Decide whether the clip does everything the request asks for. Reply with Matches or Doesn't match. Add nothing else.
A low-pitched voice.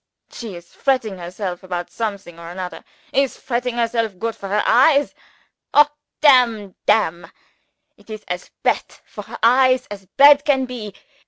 Doesn't match